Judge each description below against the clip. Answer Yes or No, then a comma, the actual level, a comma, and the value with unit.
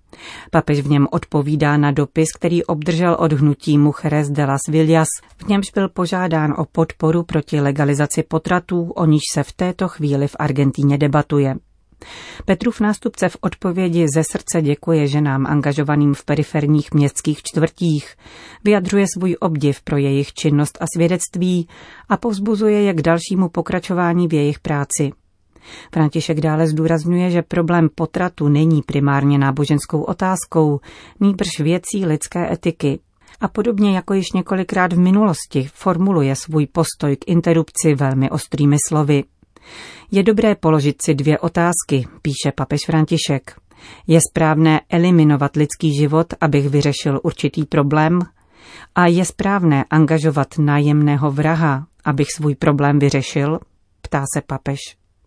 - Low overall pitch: No, medium, 160 Hz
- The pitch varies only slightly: No, average, 3.1 semitones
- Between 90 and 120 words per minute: No, average, 130 wpm